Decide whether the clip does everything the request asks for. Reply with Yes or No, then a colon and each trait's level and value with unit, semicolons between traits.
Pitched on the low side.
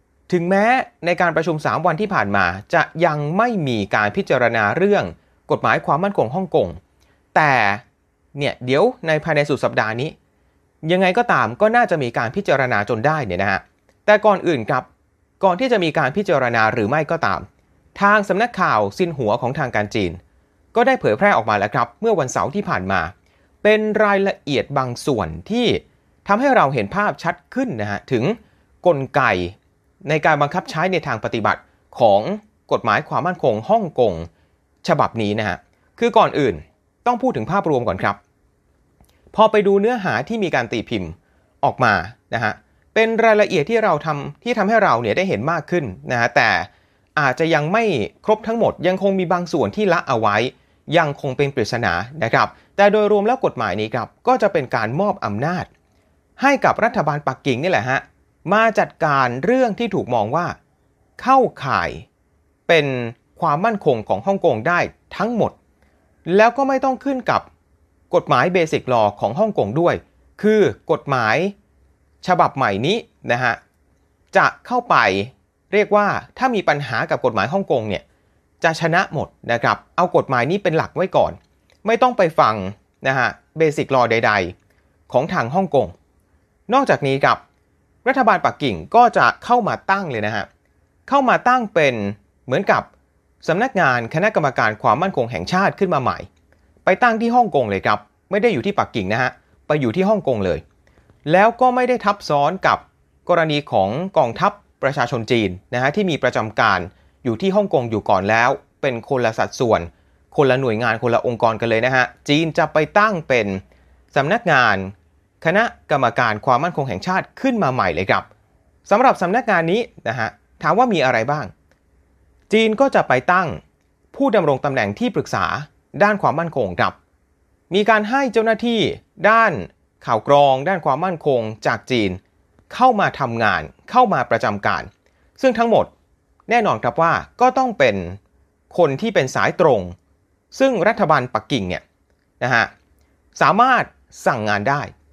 No: medium, 155 Hz